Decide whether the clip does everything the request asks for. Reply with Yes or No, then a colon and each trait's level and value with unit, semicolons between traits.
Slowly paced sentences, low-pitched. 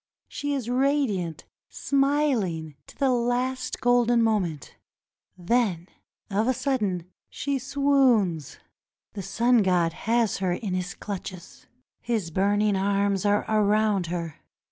No: slow, 120 wpm; high, 210 Hz